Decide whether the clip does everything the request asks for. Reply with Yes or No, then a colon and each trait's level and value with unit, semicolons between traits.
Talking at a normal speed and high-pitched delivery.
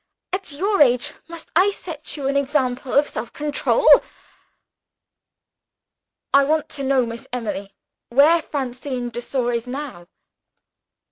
No: slow, 130 wpm; very high, 275 Hz